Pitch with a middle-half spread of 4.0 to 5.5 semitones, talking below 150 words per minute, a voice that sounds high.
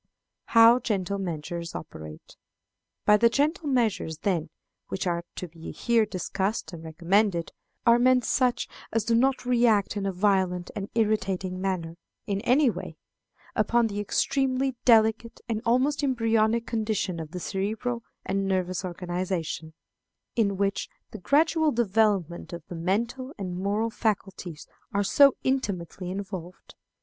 Yes: average, 4.4 semitones; average, 140 wpm; high, 205 Hz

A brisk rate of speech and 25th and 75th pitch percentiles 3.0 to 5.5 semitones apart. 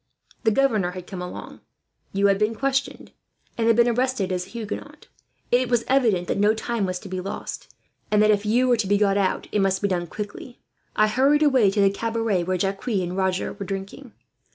Yes: fast, 215 wpm; average, 3.5 semitones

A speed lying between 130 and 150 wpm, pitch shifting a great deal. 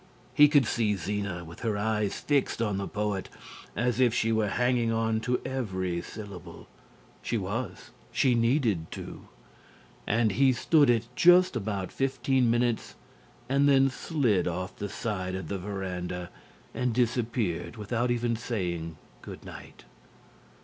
No: average, 140 wpm; average, 4.2 semitones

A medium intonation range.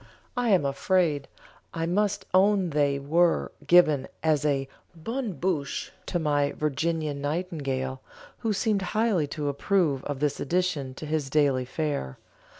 Yes: average, 4.5 semitones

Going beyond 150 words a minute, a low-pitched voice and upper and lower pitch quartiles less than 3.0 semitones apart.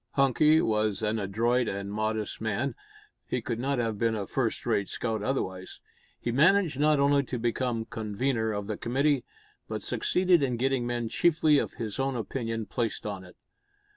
No: average, 170 wpm; low, 120 Hz; average, 4.0 semitones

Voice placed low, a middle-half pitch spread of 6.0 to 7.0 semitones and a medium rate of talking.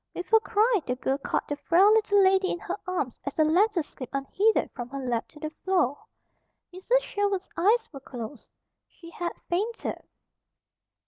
No: very high, 355 Hz; wide, 6.6 semitones; average, 175 wpm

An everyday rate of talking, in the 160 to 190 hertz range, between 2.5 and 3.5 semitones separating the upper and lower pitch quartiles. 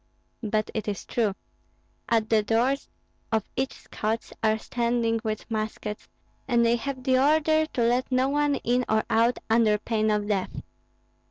No: average, 160 wpm; high, 230 Hz; average, 2.9 semitones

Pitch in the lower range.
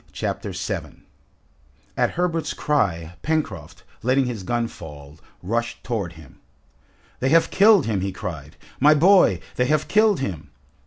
Yes: low, 115 Hz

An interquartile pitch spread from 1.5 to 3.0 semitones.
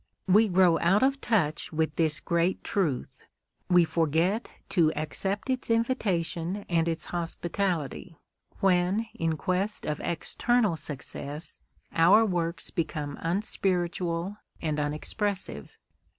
No: average, 3.6 semitones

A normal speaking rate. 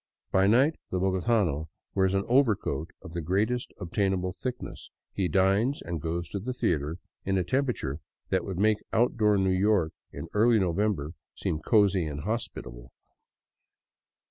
Yes: average, 145 wpm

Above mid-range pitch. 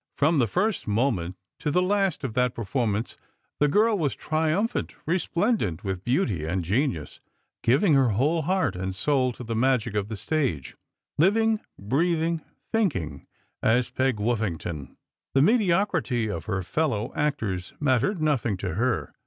No: low, 130 Hz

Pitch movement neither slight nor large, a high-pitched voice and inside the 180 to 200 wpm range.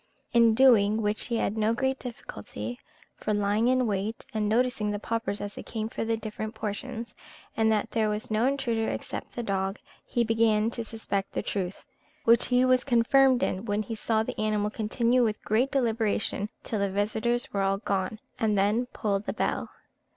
No: narrow, 2.3 semitones; high, 220 Hz; average, 190 wpm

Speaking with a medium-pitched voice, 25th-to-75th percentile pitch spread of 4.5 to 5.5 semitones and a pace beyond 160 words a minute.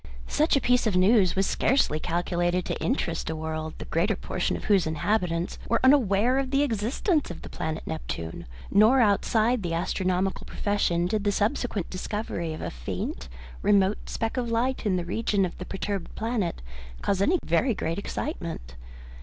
No: high, 195 Hz; average, 5.0 semitones; average, 170 wpm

